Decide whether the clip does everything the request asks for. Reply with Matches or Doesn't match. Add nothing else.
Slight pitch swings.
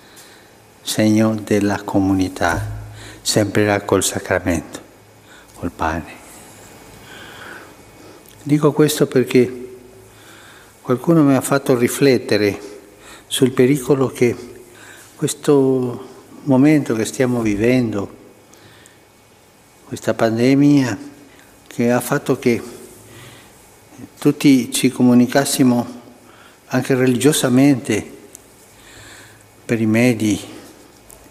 Doesn't match